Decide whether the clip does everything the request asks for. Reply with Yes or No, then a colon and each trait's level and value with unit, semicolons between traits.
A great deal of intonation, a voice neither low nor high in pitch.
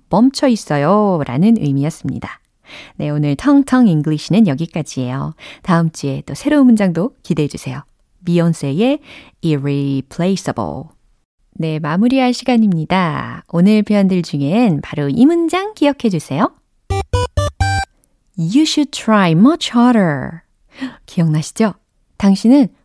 Yes: wide, 8.4 semitones; medium, 175 Hz